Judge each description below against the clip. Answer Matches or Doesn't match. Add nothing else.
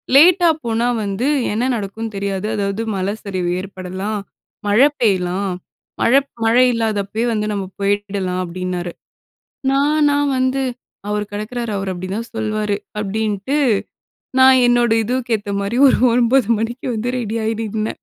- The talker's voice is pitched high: Matches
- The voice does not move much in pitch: Doesn't match